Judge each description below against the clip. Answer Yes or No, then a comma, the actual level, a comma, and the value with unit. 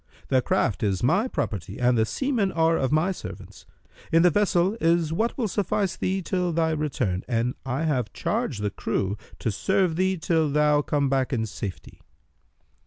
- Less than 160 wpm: No, average, 175 wpm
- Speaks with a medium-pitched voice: Yes, medium, 155 Hz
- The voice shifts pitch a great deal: Yes, wide, 7.0 semitones